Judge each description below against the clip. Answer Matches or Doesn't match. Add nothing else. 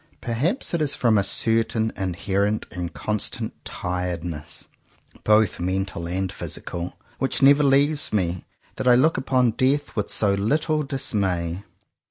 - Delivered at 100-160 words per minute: Matches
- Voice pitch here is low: Matches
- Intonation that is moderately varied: Doesn't match